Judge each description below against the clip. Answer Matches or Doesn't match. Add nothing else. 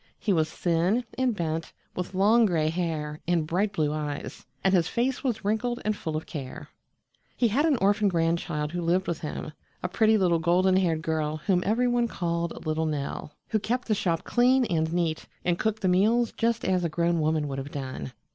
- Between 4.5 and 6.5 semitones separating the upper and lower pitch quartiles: Matches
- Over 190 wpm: Matches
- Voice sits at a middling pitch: Matches